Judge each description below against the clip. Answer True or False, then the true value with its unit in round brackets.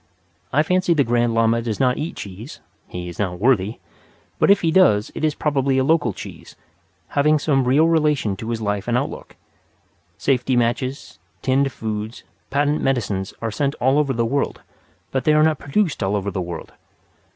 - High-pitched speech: False (130 Hz)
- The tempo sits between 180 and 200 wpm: True (185 wpm)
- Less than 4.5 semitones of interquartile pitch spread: False (5.0 semitones)